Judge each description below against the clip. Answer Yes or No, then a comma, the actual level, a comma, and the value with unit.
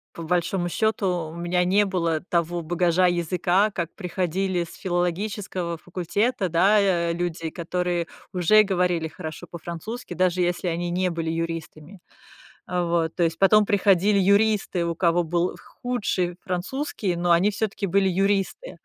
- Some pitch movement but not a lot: No, narrow, 2.3 semitones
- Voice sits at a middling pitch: Yes, medium, 180 Hz